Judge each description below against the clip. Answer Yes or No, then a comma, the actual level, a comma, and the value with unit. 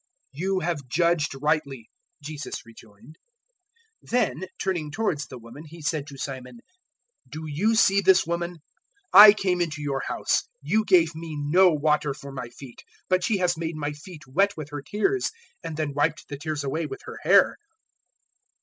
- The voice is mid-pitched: Yes, medium, 155 Hz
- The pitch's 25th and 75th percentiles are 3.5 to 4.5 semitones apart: Yes, average, 3.8 semitones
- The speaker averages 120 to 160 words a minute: No, average, 170 wpm